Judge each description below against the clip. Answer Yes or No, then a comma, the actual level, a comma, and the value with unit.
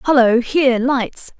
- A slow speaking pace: Yes, slow, 130 wpm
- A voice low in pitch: No, very high, 255 Hz